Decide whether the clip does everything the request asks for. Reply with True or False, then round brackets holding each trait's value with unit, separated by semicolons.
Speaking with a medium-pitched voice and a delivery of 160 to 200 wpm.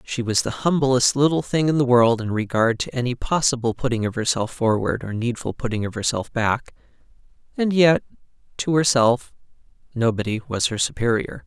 False (125 Hz; 165 wpm)